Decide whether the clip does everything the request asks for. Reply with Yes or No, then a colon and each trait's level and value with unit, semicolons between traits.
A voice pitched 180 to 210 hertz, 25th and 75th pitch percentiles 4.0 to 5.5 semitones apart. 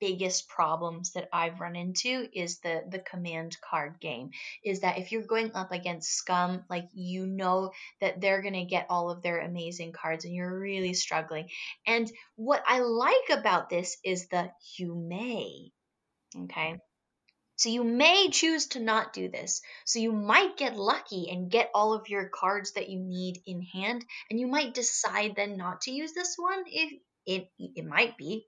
Yes: high, 190 Hz; average, 4.3 semitones